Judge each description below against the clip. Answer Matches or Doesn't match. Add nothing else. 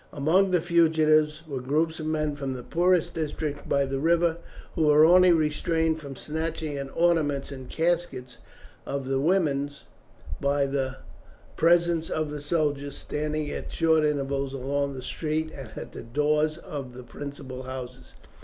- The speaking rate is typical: Matches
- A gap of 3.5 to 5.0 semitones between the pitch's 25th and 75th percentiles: Doesn't match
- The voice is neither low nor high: Matches